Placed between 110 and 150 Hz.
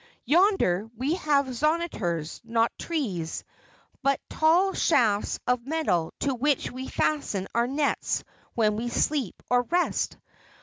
No: very high, 260 Hz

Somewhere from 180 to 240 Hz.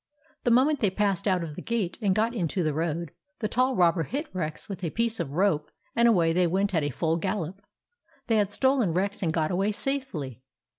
Yes: high, 190 Hz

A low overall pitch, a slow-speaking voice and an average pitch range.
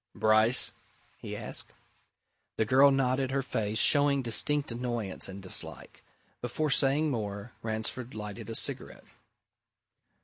Yes: low, 120 Hz; slow, 115 wpm; average, 3.8 semitones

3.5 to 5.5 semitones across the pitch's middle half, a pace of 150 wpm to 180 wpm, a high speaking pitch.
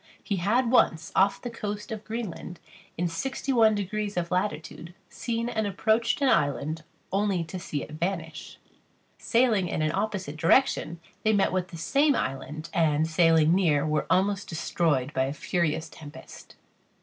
No: average, 5.0 semitones; average, 160 wpm; medium, 180 Hz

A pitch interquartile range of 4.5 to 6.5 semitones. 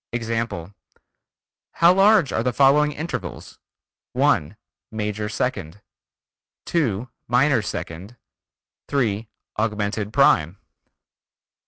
Yes: average, 5.2 semitones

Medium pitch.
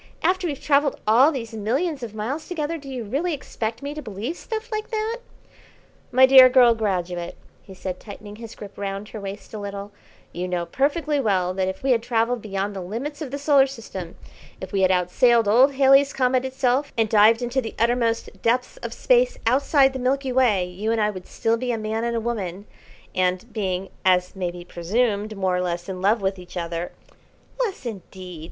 No: high, 225 Hz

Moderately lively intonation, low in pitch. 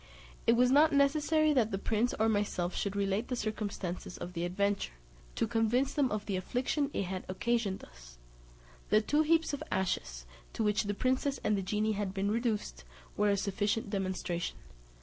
No: average, 4.4 semitones; high, 210 Hz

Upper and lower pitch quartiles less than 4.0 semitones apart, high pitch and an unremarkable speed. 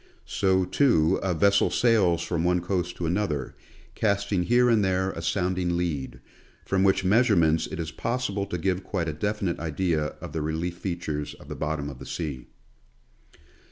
No: average, 3.4 semitones; very low, 90 Hz; average, 175 wpm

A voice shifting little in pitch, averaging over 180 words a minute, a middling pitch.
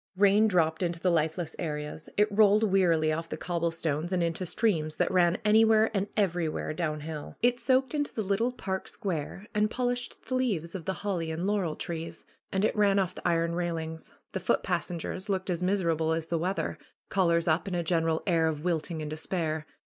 No: average, 3.5 semitones; average, 195 wpm; medium, 175 Hz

